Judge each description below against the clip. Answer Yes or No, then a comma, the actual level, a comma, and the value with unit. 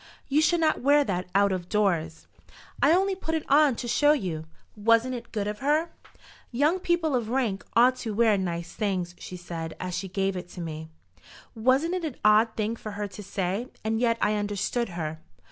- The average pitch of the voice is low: No, high, 215 Hz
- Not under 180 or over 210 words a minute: Yes, average, 195 wpm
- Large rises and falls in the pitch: Yes, wide, 6.2 semitones